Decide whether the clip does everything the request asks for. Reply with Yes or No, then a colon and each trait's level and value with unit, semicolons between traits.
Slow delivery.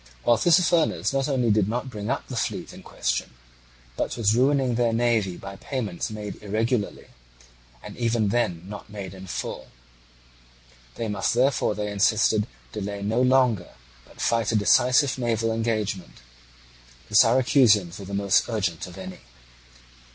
No: average, 150 wpm